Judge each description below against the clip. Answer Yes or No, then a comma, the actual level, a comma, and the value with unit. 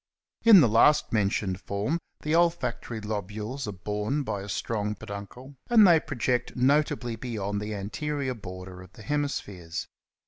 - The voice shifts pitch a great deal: Yes, wide, 5.8 semitones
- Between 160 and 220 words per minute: No, average, 150 wpm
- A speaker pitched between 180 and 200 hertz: No, low, 110 Hz